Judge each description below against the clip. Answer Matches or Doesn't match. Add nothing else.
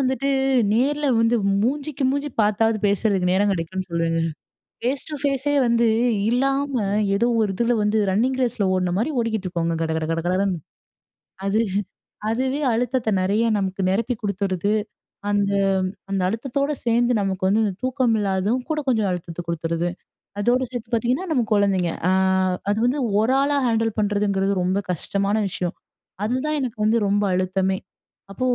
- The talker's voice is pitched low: Doesn't match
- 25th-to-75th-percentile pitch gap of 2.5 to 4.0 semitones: Doesn't match